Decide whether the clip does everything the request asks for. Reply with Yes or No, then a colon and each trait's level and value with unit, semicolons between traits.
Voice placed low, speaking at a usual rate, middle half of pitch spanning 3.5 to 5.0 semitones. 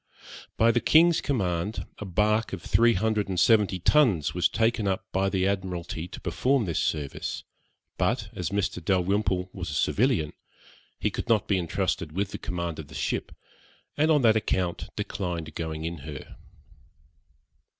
Yes: very low, 95 Hz; average, 160 wpm; average, 4.1 semitones